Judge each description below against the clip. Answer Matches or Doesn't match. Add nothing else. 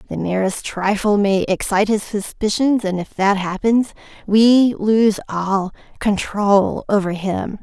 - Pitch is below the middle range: Doesn't match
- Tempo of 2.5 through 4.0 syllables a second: Matches